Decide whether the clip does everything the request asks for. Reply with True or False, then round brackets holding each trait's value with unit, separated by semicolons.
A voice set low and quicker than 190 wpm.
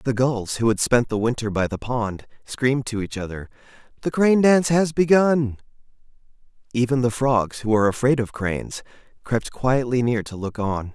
False (120 Hz; 180 wpm)